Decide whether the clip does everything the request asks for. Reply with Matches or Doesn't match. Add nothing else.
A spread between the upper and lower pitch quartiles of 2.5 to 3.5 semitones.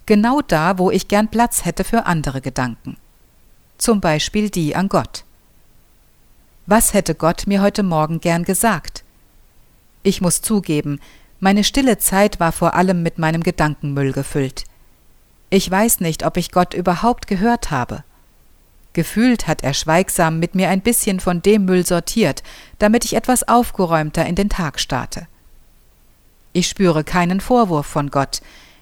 Doesn't match